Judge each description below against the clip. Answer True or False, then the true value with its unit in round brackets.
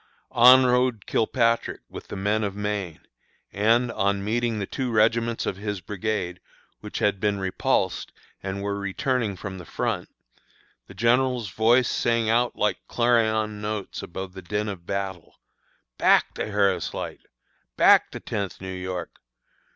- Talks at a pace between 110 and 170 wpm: True (150 wpm)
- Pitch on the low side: True (105 Hz)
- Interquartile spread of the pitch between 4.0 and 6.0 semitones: False (3.1 semitones)